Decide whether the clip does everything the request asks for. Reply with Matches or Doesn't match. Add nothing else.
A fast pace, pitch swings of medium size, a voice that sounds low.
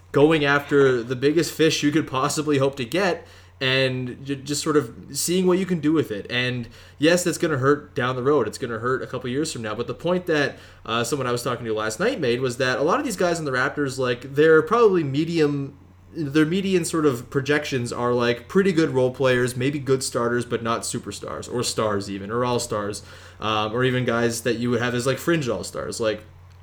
Matches